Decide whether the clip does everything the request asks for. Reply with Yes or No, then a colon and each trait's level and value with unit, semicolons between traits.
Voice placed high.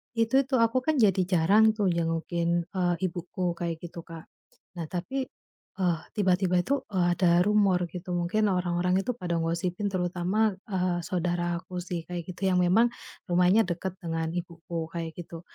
No: medium, 180 Hz